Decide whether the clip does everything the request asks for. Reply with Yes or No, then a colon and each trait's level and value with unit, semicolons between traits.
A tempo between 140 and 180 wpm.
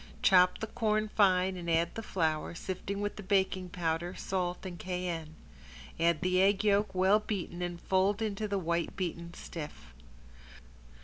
Yes: average, 160 wpm